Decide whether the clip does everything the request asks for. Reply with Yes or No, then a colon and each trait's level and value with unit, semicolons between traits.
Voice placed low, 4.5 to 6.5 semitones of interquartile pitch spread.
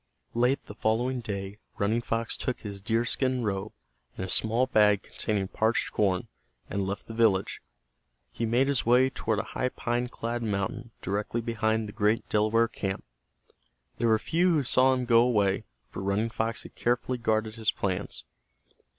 No: low, 110 Hz; narrow, 2.6 semitones